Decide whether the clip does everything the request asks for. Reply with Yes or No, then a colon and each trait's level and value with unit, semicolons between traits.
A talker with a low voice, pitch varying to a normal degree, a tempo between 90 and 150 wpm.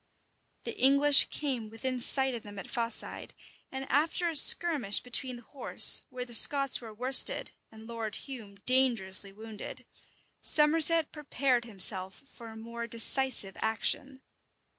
No: high, 245 Hz; average, 3.7 semitones; average, 140 wpm